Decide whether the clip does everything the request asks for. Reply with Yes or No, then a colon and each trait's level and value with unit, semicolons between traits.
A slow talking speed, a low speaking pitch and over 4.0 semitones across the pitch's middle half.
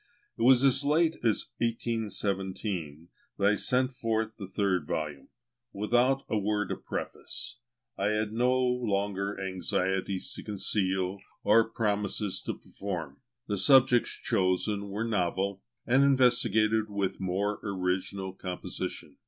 No: slow, 125 wpm; low, 105 Hz; average, 3.3 semitones